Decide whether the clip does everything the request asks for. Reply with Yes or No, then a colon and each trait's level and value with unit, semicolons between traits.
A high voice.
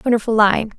Yes: high, 220 Hz